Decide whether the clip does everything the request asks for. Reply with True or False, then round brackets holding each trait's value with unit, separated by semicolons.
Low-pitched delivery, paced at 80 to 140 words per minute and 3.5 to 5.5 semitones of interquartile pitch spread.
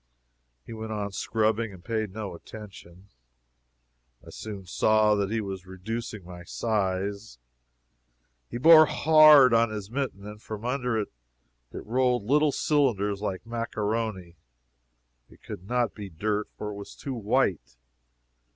False (110 Hz; 135 wpm; 2.9 semitones)